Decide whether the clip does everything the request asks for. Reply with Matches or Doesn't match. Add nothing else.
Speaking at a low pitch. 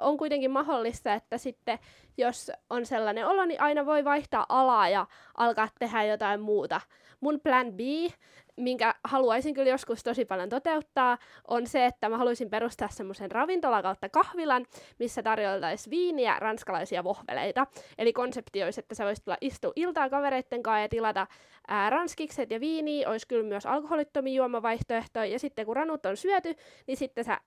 Doesn't match